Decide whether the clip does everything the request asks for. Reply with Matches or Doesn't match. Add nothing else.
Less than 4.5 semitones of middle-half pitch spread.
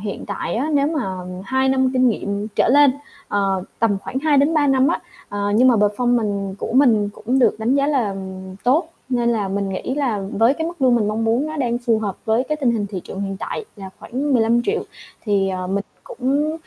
Doesn't match